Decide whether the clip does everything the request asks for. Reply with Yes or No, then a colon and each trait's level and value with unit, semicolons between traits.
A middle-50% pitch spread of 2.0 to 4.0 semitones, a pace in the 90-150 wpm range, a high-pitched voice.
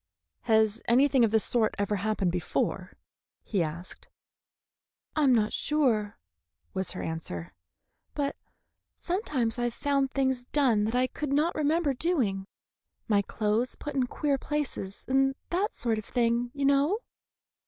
No: average, 4.9 semitones; average, 145 wpm; high, 245 Hz